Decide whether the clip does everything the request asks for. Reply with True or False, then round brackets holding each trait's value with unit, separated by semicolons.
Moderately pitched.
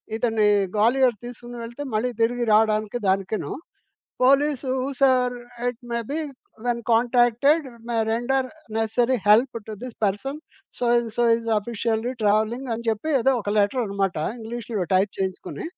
False (235 Hz)